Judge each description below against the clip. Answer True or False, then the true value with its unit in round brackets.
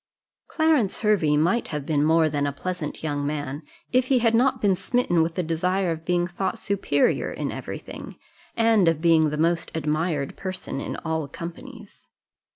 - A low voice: False (170 Hz)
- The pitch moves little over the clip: False (4.6 semitones)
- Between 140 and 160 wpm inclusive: False (175 wpm)